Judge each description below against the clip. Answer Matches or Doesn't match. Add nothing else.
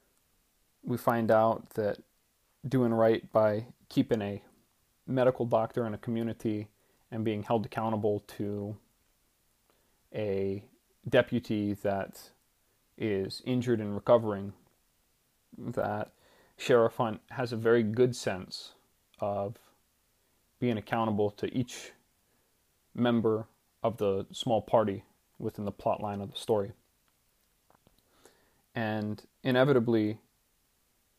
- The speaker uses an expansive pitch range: Doesn't match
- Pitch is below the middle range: Matches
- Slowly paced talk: Matches